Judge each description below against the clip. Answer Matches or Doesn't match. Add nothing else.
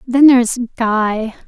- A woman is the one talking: Matches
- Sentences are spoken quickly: Doesn't match